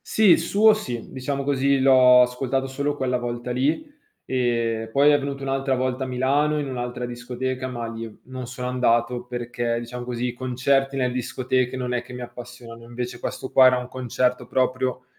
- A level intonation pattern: Yes, narrow, 1.5 semitones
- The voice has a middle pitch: No, low, 125 Hz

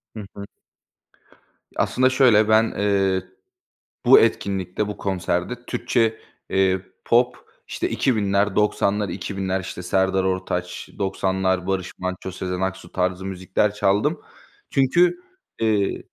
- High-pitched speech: No, very low, 95 Hz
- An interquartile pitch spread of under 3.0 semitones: Yes, narrow, 2.5 semitones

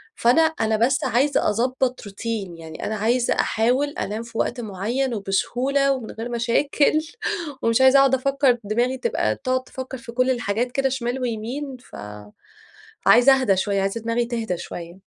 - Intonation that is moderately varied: Yes, average, 3.3 semitones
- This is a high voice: Yes, high, 240 Hz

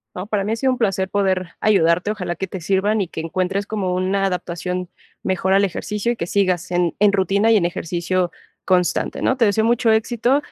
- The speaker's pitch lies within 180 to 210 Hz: Yes, high, 190 Hz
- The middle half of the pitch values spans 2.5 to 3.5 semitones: Yes, average, 2.8 semitones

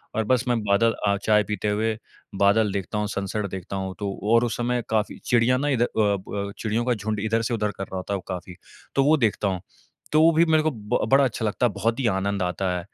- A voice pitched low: Yes, low, 105 Hz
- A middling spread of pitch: Yes, average, 3.0 semitones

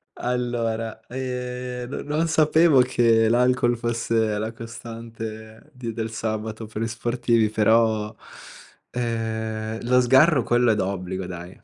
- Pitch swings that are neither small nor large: No, narrow, 2.0 semitones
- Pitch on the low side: Yes, low, 115 Hz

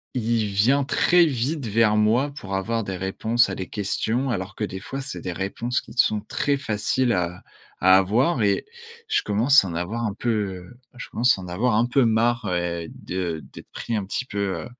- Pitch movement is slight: No, average, 4.1 semitones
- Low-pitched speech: Yes, low, 110 Hz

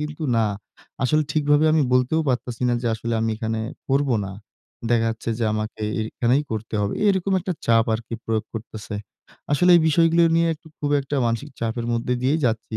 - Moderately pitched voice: No, low, 120 Hz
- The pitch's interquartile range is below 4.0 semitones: No, average, 5.0 semitones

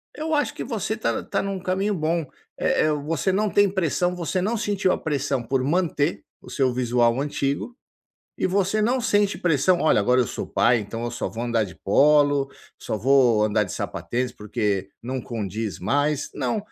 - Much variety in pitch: Yes, wide, 7.7 semitones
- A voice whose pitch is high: No, medium, 145 Hz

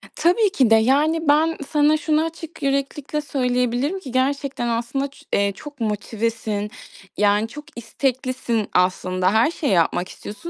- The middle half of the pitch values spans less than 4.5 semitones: No, average, 5.2 semitones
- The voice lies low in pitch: No, very high, 260 Hz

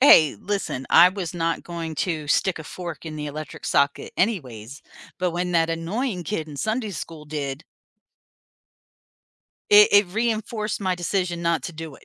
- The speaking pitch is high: No, medium, 170 Hz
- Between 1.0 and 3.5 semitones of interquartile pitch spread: No, average, 4.2 semitones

